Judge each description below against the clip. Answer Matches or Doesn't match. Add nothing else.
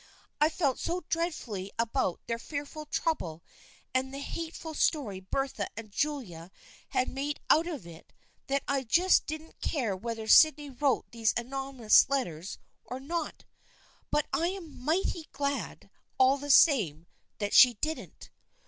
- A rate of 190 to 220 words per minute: Doesn't match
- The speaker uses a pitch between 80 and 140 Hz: Doesn't match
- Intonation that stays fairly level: Doesn't match